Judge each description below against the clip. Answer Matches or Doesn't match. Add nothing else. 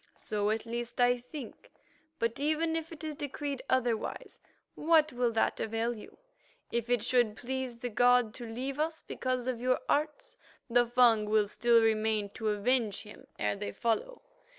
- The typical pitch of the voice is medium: Doesn't match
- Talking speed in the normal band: Matches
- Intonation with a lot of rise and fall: Doesn't match